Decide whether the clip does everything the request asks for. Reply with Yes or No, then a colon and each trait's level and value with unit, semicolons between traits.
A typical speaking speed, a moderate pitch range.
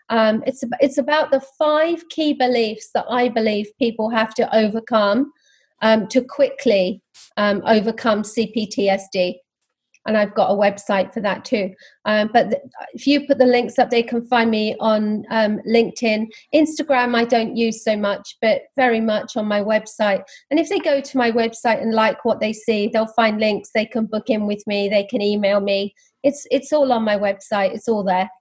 Yes: average, 190 wpm; average, 3.2 semitones